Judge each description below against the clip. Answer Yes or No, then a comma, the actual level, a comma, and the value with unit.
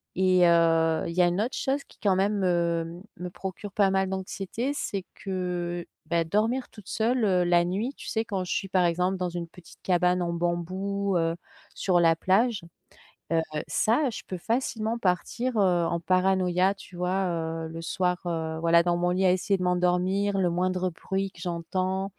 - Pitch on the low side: No, medium, 185 Hz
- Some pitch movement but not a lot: No, narrow, 2.1 semitones